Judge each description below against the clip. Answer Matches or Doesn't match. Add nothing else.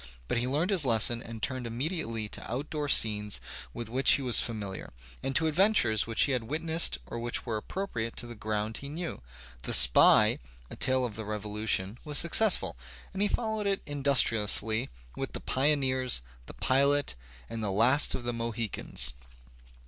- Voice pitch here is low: Matches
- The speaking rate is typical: Matches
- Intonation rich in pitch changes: Doesn't match